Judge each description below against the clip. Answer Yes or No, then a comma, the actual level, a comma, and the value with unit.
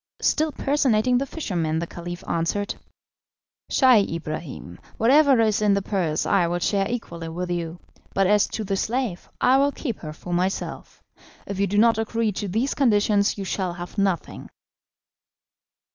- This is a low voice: No, high, 200 Hz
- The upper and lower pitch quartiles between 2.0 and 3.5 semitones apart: No, average, 4.6 semitones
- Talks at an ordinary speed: Yes, average, 160 wpm